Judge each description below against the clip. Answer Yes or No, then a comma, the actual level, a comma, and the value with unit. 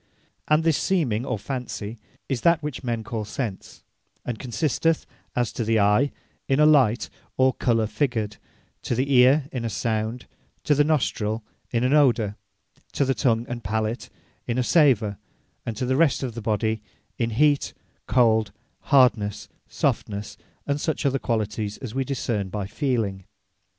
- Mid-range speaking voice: No, low, 120 Hz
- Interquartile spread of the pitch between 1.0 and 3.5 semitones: No, average, 4.0 semitones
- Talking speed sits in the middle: Yes, average, 160 wpm